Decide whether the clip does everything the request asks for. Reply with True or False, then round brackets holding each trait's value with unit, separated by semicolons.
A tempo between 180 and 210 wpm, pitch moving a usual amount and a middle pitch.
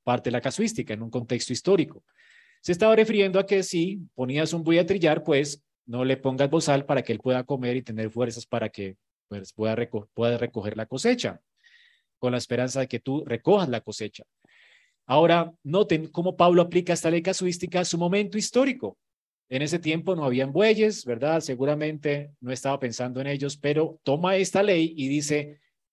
False (185 wpm; 6.6 semitones; 150 Hz)